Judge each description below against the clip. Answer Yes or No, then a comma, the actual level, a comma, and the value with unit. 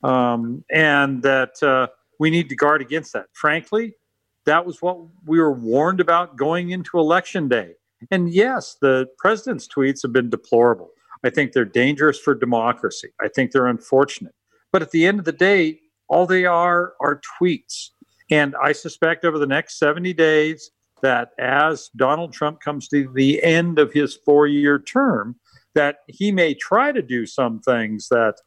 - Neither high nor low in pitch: Yes, medium, 150 Hz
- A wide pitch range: No, average, 4.3 semitones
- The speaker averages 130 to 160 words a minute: No, average, 170 wpm